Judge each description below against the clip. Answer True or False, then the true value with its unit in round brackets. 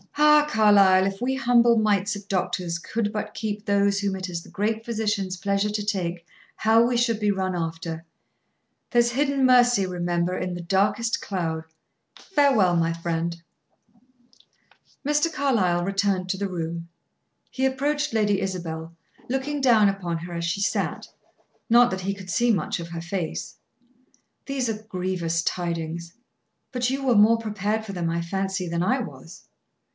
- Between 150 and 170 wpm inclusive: True (160 wpm)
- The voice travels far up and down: False (4.8 semitones)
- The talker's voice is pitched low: False (200 Hz)